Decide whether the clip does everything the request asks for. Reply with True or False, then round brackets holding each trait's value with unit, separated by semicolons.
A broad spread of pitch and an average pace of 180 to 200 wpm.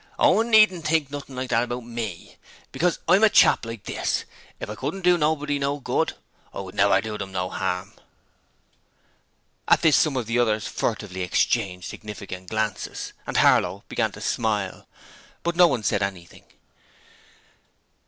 False (6.6 semitones; 160 wpm)